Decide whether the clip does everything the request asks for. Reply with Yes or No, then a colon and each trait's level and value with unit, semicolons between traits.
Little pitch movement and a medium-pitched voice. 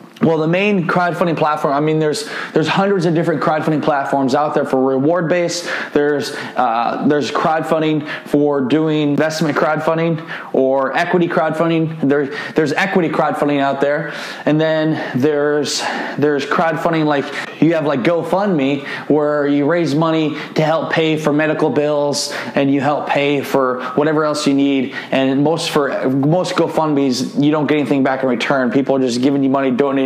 Yes: narrow, 2.1 semitones; medium, 150 Hz